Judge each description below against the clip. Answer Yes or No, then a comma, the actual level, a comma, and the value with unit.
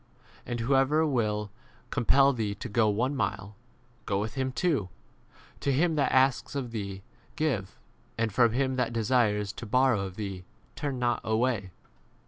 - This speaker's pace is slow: No, average, 160 wpm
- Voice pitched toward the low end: Yes, low, 120 Hz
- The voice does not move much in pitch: No, average, 4.2 semitones